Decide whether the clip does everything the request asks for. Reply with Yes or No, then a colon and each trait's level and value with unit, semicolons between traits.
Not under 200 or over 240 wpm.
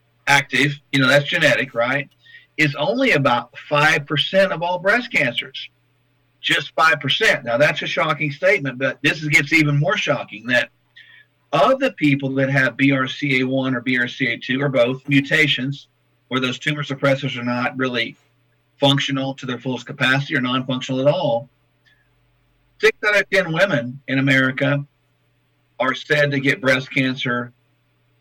No: average, 145 wpm